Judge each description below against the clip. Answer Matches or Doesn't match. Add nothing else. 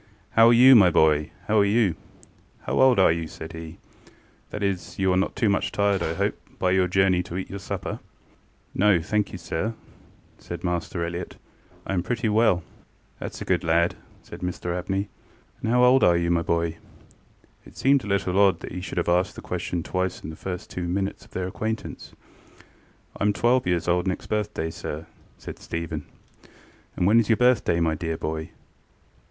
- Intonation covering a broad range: Doesn't match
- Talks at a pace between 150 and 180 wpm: Doesn't match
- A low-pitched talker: Matches